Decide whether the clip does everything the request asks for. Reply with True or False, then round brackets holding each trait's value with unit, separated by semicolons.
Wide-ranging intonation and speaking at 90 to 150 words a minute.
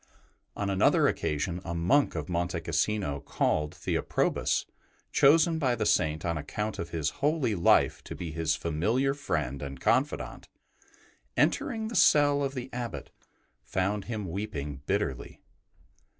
True (8.6 semitones; 135 wpm)